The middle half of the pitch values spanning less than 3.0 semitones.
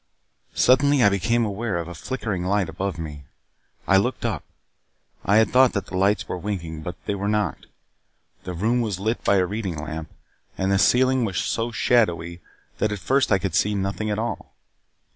No: average, 4.0 semitones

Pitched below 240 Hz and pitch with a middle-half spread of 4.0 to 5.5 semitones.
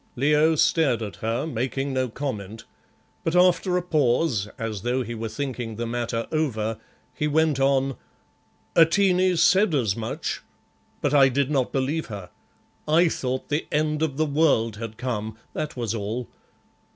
Yes: low, 135 Hz; average, 5.2 semitones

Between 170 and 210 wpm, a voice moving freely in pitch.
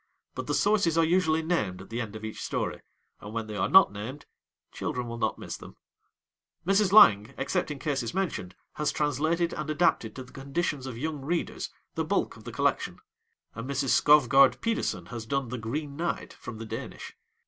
Yes: average, 190 wpm; wide, 6.1 semitones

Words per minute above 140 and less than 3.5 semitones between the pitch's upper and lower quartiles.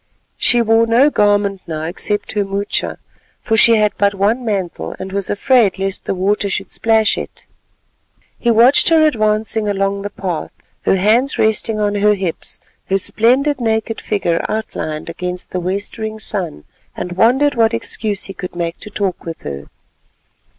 Yes: average, 165 wpm; average, 2.8 semitones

